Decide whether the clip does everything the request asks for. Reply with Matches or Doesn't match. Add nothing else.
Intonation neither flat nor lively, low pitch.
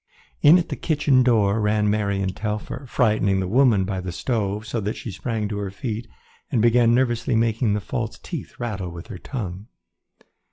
Matches